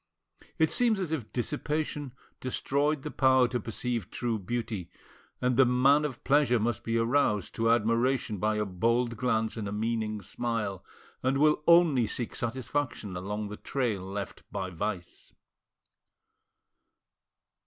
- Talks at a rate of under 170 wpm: Yes, average, 140 wpm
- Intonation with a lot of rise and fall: No, average, 4.0 semitones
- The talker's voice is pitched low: Yes, low, 120 Hz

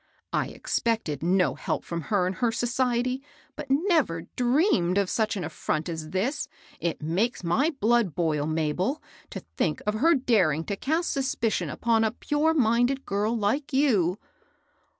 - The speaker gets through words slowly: No, average, 160 wpm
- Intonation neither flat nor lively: No, wide, 7.2 semitones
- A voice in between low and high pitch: No, high, 220 Hz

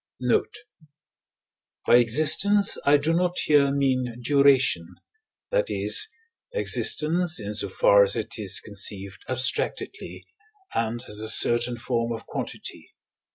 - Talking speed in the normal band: No, slow, 120 wpm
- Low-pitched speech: Yes, low, 125 Hz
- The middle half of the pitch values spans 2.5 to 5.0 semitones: No, wide, 5.5 semitones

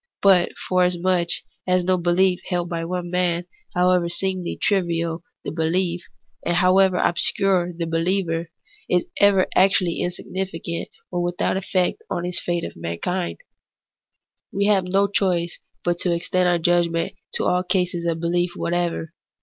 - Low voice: No, medium, 175 Hz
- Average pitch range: No, narrow, 1.4 semitones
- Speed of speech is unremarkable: Yes, average, 145 wpm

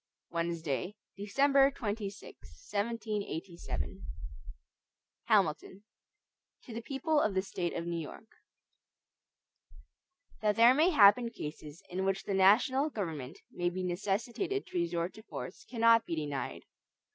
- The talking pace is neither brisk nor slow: No, slow, 120 wpm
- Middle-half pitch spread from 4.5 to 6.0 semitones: Yes, average, 5.1 semitones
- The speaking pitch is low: No, high, 200 Hz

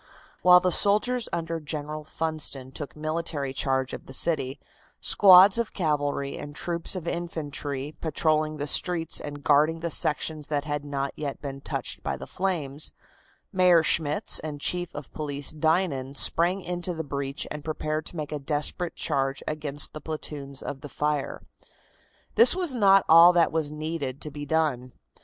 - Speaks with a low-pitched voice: No, medium, 155 Hz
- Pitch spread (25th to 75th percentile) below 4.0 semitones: Yes, average, 2.8 semitones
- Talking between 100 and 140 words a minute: No, average, 165 wpm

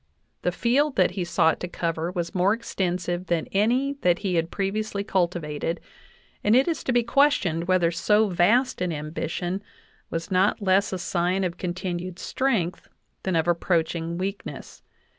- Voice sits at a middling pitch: Yes, medium, 180 Hz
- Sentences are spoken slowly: No, average, 160 wpm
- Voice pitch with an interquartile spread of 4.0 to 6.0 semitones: No, average, 3.4 semitones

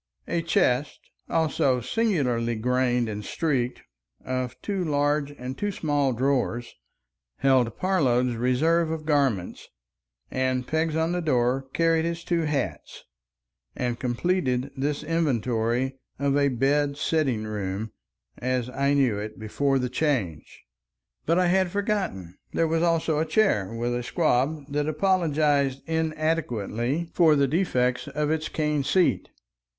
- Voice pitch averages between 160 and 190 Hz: No, medium, 140 Hz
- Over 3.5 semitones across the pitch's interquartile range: Yes, average, 4.5 semitones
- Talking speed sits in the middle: No, slow, 130 wpm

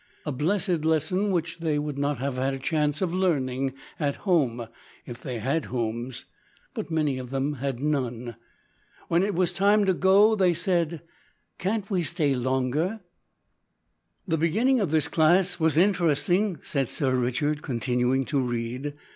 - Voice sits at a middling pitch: Yes, medium, 150 Hz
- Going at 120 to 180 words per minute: Yes, average, 155 wpm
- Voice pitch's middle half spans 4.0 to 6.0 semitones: Yes, average, 5.2 semitones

